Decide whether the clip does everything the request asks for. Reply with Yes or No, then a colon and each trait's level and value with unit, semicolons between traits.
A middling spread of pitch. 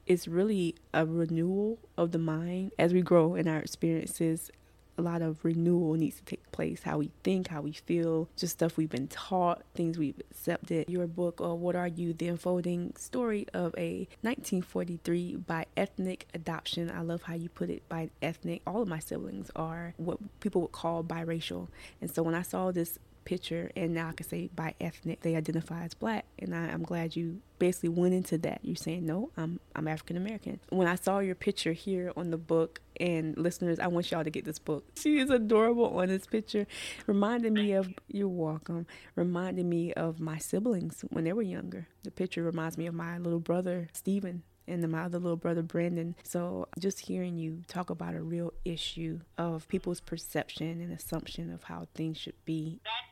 No: narrow, 1.7 semitones